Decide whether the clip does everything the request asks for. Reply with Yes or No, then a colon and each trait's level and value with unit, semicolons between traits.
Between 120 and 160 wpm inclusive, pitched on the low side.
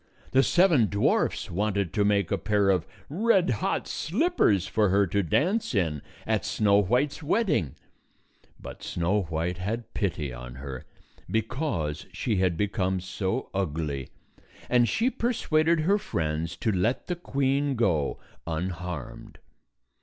Yes: slow, 135 wpm; low, 100 Hz